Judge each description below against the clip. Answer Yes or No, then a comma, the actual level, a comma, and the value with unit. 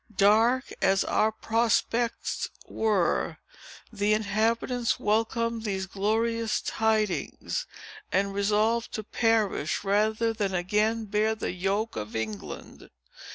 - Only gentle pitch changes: Yes, narrow, 2.3 semitones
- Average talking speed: No, slow, 105 wpm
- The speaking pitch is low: No, high, 215 Hz